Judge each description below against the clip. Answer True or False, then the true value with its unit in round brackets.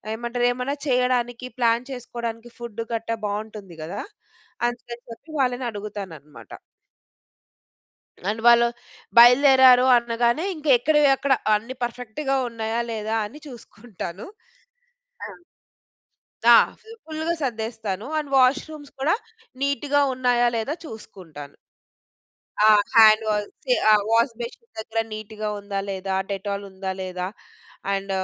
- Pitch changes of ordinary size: True (3.2 semitones)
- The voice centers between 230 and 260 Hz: True (235 Hz)